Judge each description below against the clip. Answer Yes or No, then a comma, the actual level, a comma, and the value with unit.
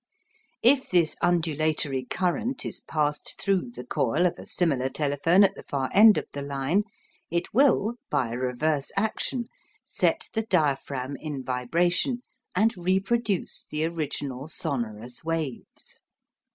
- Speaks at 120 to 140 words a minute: Yes, slow, 135 wpm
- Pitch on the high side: No, medium, 160 Hz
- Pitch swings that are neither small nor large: No, wide, 5.8 semitones